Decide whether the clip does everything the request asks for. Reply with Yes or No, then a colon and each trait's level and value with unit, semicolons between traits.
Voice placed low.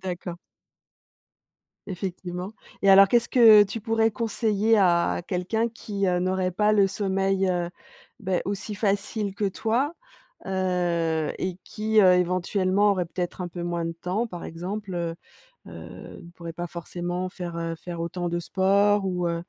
No: medium, 185 Hz